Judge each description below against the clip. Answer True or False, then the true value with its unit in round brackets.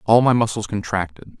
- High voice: False (105 Hz)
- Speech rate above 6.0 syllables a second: False (5.5 syllables/s)